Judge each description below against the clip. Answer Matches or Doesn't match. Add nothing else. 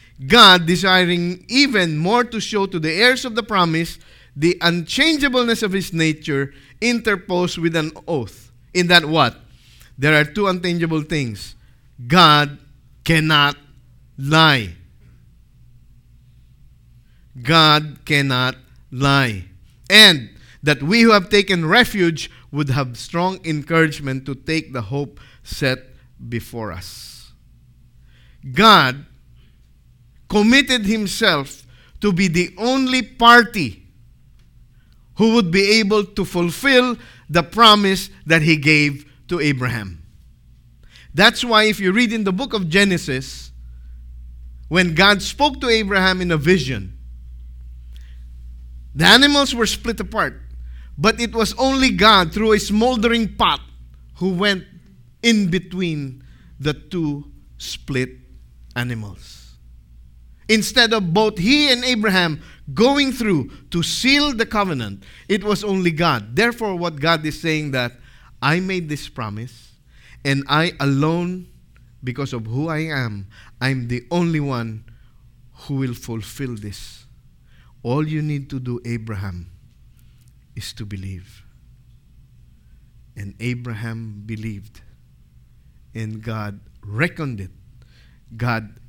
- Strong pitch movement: Matches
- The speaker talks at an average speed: Doesn't match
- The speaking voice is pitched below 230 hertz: Matches